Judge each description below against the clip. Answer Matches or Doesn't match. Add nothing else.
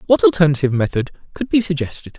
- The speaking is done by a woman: Doesn't match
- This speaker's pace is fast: Doesn't match